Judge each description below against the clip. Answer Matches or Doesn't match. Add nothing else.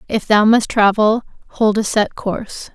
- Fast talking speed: Doesn't match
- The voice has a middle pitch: Doesn't match